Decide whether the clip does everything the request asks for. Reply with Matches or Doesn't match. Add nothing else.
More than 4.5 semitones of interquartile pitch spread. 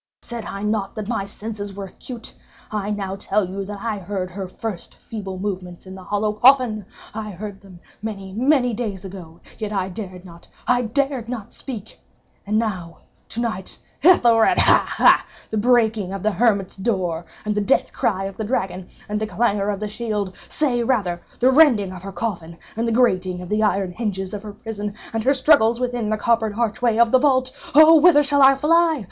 Doesn't match